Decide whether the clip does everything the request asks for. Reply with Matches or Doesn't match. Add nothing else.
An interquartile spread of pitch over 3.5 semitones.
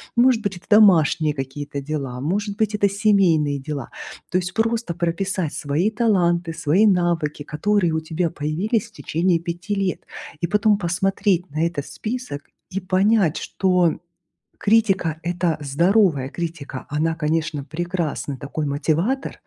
Matches